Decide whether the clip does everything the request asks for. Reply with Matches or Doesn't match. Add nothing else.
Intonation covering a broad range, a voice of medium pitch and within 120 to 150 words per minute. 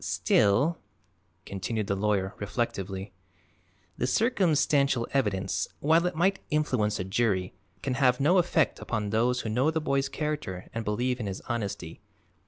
Doesn't match